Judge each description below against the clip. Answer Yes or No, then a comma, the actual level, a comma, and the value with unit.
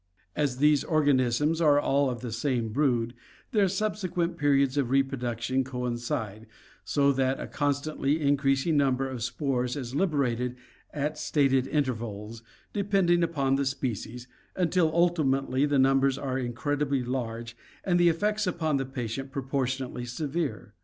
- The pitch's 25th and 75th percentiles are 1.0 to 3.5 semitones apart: Yes, average, 3.2 semitones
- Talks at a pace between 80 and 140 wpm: Yes, slow, 135 wpm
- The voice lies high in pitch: No, low, 135 Hz